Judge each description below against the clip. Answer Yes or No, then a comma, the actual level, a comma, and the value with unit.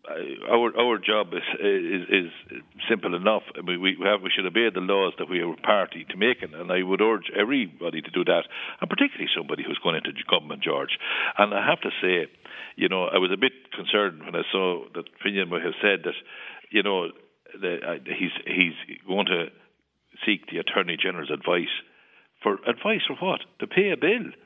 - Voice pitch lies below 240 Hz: No, very high, 275 Hz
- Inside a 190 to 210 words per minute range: Yes, average, 200 wpm